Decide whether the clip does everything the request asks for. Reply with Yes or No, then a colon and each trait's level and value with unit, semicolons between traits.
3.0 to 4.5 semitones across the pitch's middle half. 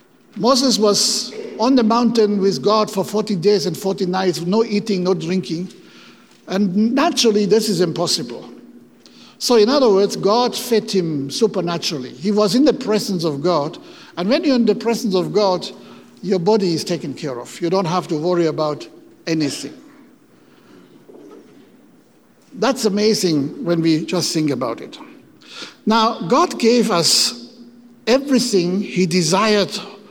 Yes: average, 4.2 semitones